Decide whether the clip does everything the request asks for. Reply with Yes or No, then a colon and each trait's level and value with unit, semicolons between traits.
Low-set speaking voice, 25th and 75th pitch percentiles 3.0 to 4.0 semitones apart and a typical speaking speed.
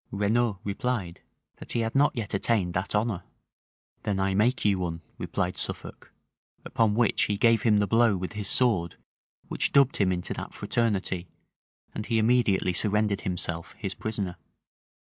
Yes: low, 105 Hz; average, 3.3 semitones; average, 160 wpm